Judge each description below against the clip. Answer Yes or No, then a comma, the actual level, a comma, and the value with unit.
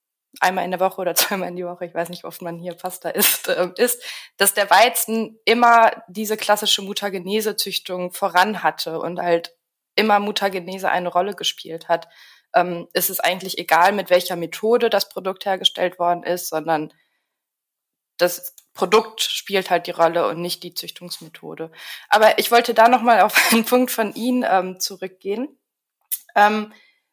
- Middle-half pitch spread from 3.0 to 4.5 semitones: Yes, average, 3.5 semitones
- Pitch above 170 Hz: Yes, high, 190 Hz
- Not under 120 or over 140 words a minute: No, average, 165 wpm